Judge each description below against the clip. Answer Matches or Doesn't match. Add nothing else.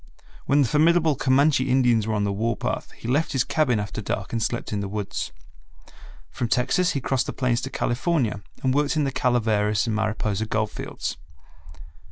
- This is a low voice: Matches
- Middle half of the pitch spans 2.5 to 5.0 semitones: Matches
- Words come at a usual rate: Matches